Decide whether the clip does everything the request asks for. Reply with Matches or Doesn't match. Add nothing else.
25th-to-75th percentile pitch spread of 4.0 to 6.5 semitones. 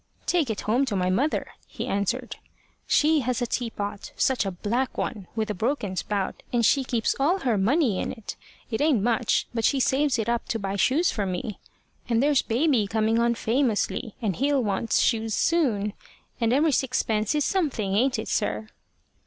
Matches